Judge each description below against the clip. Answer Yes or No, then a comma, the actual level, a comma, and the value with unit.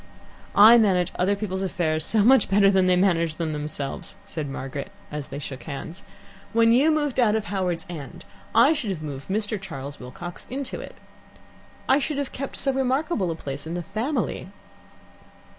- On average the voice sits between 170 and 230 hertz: Yes, high, 190 Hz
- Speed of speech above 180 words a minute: No, average, 175 wpm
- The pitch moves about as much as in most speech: No, wide, 6.5 semitones